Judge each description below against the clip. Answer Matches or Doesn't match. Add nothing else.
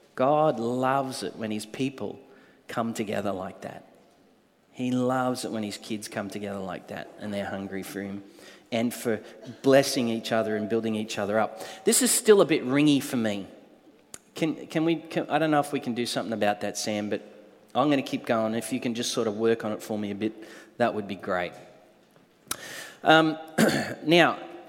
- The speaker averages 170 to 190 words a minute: Doesn't match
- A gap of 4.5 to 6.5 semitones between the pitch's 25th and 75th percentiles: Doesn't match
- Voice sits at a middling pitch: Doesn't match